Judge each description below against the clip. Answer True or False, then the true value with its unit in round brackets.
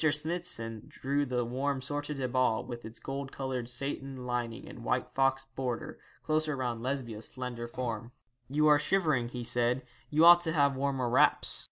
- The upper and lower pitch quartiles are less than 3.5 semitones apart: True (2.9 semitones)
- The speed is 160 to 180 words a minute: True (170 wpm)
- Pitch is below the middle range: True (130 Hz)